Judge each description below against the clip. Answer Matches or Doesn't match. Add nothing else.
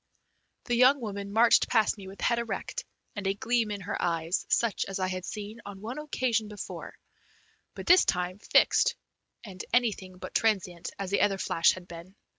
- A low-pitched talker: Doesn't match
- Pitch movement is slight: Doesn't match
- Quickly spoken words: Doesn't match